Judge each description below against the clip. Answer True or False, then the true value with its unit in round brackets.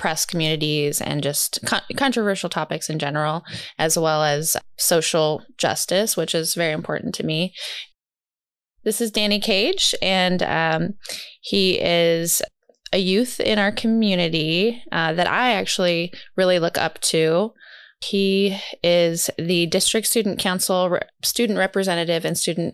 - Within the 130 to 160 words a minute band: True (135 wpm)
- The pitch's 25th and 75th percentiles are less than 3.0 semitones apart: False (3.7 semitones)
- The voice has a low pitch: False (175 Hz)